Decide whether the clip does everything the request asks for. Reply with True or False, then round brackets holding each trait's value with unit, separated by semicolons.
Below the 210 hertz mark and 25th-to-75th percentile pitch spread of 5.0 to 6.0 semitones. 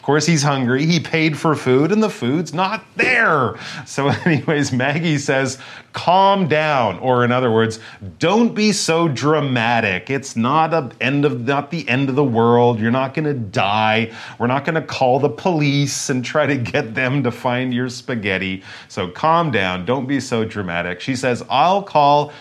False (135 Hz; 4.2 semitones)